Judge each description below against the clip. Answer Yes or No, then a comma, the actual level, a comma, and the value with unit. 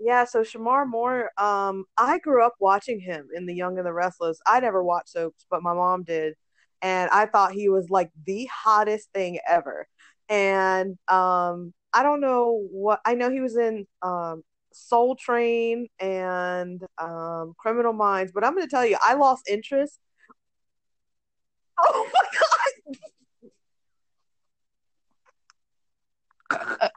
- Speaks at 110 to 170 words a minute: Yes, average, 145 wpm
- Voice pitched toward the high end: Yes, high, 200 Hz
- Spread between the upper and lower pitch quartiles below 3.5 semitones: No, average, 4.7 semitones